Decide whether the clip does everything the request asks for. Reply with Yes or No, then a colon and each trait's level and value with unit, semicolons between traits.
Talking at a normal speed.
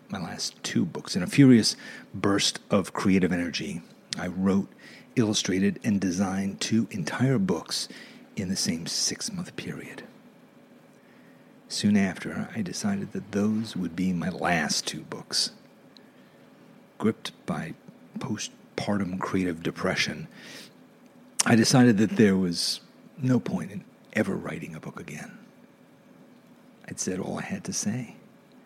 No: slow, 130 wpm